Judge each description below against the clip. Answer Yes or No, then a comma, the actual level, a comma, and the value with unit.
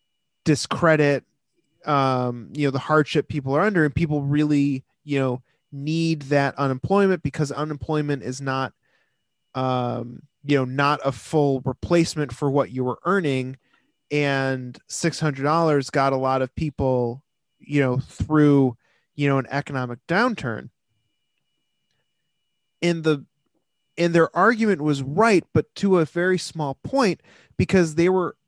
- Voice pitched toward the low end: No, medium, 145 Hz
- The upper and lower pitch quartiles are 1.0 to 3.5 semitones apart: Yes, average, 3.1 semitones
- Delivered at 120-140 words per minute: Yes, slow, 135 wpm